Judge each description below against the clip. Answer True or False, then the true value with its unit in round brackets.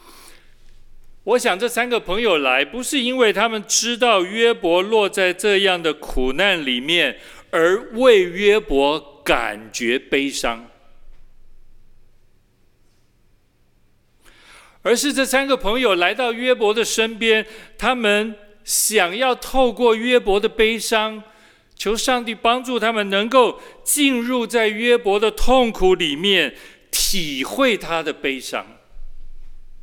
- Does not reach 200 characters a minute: True (170 characters per minute)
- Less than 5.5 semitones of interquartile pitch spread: True (5.1 semitones)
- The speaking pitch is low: False (220 Hz)